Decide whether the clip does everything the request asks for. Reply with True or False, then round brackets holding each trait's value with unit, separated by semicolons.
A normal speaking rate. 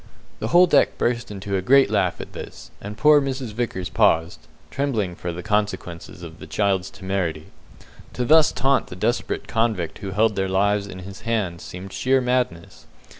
True (175 wpm)